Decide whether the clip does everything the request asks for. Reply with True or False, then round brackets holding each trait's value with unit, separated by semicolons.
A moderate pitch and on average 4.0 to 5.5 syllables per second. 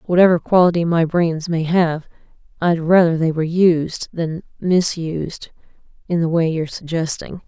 True (165 Hz; 4.7 syllables/s)